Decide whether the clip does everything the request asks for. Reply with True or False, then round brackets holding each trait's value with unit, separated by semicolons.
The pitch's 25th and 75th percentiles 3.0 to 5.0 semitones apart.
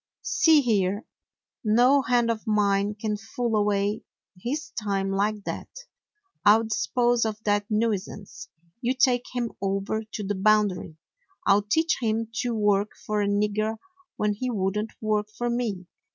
False (2.5 semitones)